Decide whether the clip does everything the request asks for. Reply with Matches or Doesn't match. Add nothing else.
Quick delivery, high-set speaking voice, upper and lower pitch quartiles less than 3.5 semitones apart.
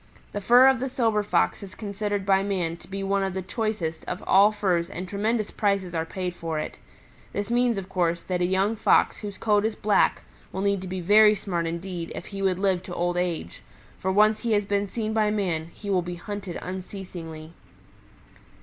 Matches